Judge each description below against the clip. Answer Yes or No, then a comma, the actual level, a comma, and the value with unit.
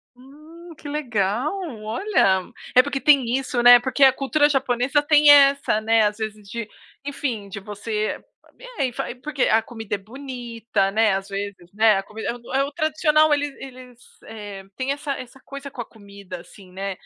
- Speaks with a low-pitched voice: No, high, 245 Hz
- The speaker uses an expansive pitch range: No, average, 5.0 semitones